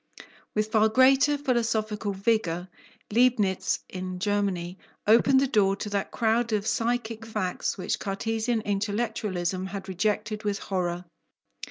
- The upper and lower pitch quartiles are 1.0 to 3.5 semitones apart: Yes, average, 2.8 semitones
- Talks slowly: Yes, slow, 125 wpm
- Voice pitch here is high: Yes, high, 210 Hz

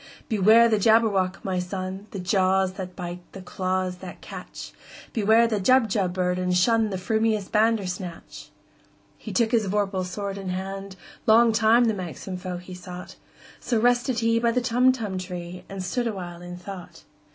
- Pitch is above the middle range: Yes, high, 195 Hz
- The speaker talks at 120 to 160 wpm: Yes, average, 140 wpm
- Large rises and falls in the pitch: No, average, 3.4 semitones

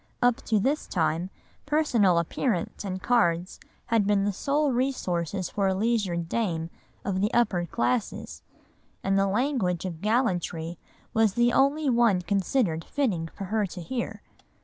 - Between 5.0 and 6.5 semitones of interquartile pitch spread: Yes, wide, 5.4 semitones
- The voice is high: Yes, high, 200 Hz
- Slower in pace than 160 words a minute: Yes, average, 150 wpm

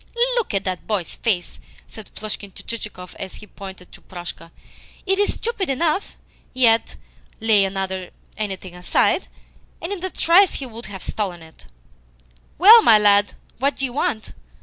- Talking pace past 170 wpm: No, average, 155 wpm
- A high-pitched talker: Yes, high, 210 Hz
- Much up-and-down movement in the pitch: Yes, wide, 6.5 semitones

